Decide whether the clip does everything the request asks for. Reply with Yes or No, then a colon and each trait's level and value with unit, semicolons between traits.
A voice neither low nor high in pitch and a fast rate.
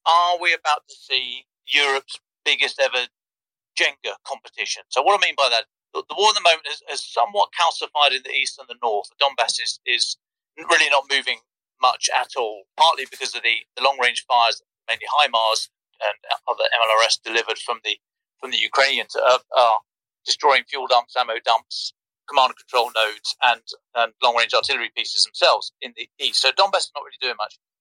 No: medium, 170 Hz; average, 185 wpm